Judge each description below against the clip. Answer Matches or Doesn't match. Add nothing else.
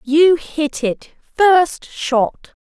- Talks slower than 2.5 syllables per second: Matches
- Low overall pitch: Doesn't match